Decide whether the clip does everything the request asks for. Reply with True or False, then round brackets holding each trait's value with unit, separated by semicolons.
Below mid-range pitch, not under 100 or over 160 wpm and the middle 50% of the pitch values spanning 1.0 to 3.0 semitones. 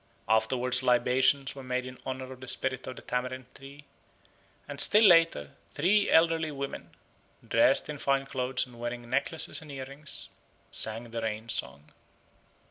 True (130 Hz; 150 wpm; 2.4 semitones)